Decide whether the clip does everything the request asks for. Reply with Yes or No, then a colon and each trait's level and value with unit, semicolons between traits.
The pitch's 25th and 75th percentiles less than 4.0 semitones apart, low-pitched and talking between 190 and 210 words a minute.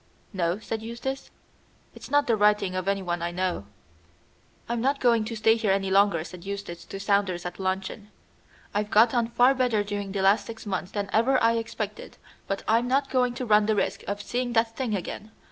No: average, 3.1 semitones; high, 210 Hz; average, 200 wpm